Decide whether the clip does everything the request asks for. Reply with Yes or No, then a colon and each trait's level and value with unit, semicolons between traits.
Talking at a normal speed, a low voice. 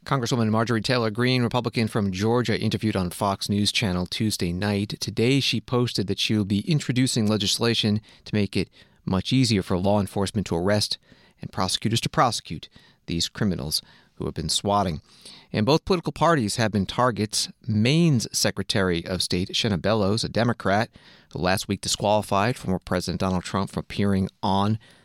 Yes: average, 165 wpm; low, 105 Hz